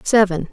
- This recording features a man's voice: No, female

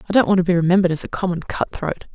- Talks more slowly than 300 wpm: No, fast, 310 wpm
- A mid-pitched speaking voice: Yes, medium, 180 Hz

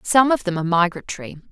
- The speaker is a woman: Yes, female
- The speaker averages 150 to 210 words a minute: Yes, average, 200 wpm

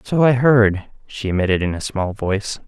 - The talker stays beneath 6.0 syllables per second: Yes, 5.0 syllables/s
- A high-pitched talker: No, low, 105 Hz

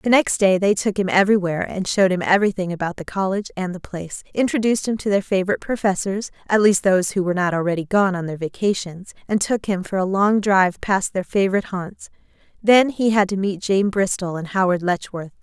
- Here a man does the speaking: No, female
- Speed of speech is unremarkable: No, fast, 215 wpm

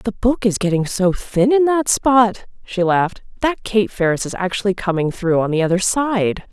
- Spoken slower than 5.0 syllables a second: Yes, 4.8 syllables/s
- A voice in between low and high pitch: No, high, 205 Hz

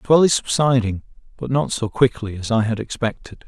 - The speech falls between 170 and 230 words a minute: Yes, fast, 205 wpm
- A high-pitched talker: No, low, 120 Hz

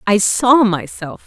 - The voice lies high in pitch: Yes, high, 205 Hz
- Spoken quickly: No, average, 140 wpm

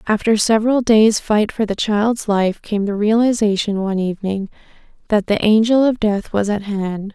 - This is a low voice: No, high, 210 Hz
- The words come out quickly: No, average, 175 wpm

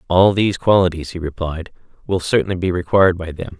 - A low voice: Yes, very low, 90 Hz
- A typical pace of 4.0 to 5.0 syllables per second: No, 6.2 syllables/s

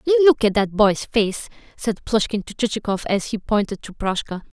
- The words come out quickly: No, average, 185 wpm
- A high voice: Yes, high, 220 Hz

